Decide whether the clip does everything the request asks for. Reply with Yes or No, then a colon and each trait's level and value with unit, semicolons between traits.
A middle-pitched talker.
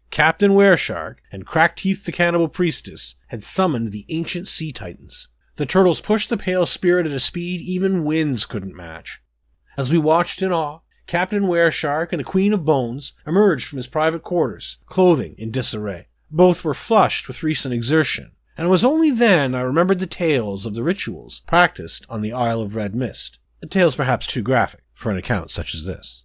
Yes: medium, 155 Hz